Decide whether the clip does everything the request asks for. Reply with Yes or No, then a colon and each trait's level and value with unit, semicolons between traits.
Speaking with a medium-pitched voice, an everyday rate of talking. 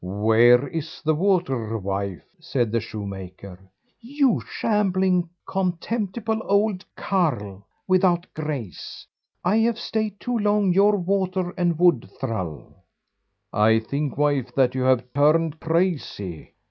No: medium, 160 Hz; slow, 120 wpm